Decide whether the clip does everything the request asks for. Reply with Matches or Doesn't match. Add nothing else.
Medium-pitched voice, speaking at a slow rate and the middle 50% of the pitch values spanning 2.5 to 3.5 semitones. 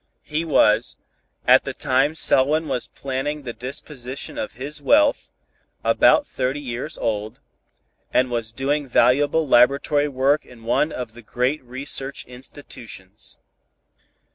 Doesn't match